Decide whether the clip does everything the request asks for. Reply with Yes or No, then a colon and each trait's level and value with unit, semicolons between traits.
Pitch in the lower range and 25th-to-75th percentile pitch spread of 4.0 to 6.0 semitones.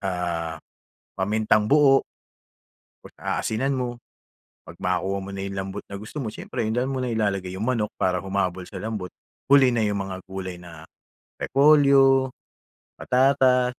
Yes: low, 105 Hz; average, 5.2 semitones